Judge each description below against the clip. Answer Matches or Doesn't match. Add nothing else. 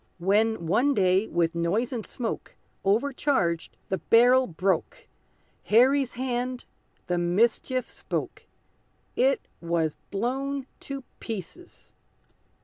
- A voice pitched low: Doesn't match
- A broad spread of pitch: Matches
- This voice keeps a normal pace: Doesn't match